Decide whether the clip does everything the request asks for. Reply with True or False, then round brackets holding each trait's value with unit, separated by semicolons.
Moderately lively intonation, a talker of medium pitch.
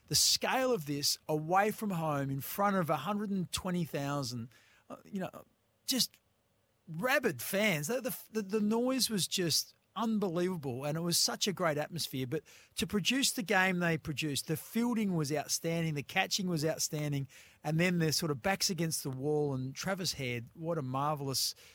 False (6.0 semitones; 165 Hz)